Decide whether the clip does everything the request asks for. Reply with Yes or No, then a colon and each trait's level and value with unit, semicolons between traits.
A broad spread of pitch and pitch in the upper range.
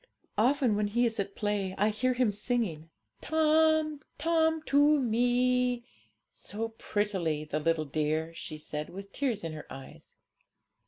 Yes: wide, 7.4 semitones; high, 220 Hz